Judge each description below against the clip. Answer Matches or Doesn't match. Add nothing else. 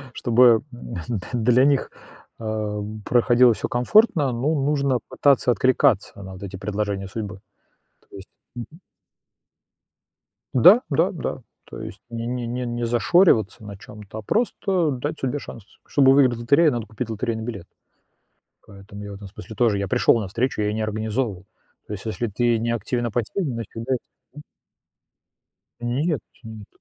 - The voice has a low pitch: Matches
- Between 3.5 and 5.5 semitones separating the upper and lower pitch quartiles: Matches